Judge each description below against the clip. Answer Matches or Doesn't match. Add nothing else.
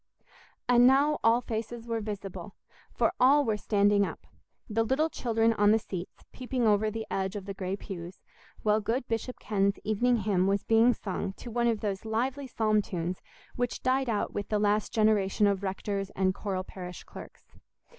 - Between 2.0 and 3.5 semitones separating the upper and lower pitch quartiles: Matches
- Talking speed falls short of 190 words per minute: Matches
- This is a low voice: Doesn't match